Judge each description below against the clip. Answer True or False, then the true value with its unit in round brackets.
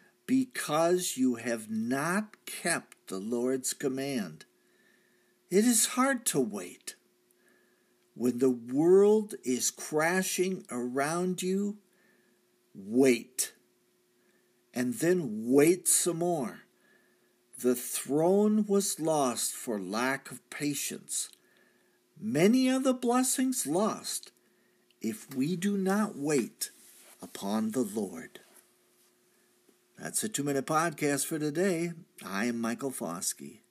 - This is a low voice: False (155 Hz)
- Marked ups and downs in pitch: True (7.9 semitones)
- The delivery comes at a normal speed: False (105 wpm)